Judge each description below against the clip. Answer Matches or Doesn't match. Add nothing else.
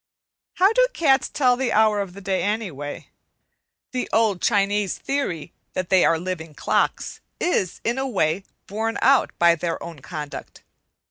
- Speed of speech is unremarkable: Matches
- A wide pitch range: Matches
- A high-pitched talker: Matches